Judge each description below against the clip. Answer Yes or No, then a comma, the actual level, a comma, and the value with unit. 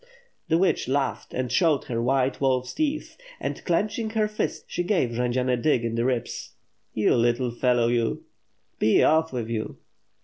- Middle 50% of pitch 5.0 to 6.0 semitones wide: Yes, wide, 5.4 semitones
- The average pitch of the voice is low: Yes, low, 130 Hz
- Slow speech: No, average, 170 wpm